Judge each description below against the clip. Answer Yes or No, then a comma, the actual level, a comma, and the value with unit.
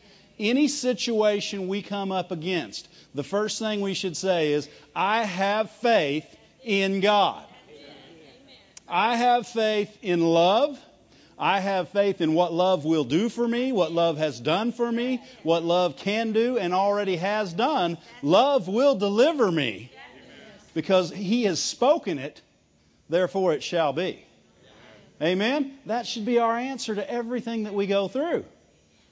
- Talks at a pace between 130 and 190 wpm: Yes, average, 150 wpm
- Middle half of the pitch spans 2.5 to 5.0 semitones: Yes, average, 4.5 semitones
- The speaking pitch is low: No, high, 205 Hz